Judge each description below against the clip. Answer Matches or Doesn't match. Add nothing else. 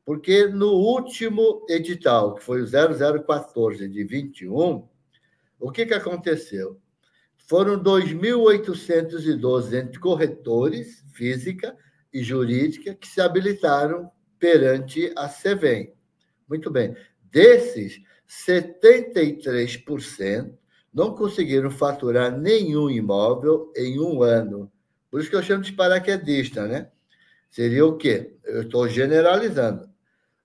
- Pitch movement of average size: Doesn't match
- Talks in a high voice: Doesn't match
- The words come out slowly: Matches